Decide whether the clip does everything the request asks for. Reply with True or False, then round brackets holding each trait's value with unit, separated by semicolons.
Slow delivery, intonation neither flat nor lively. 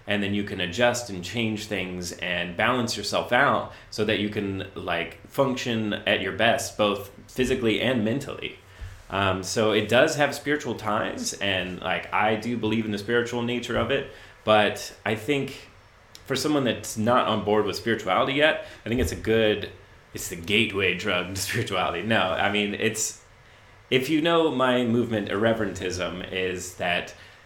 False (170 wpm; 3.5 semitones)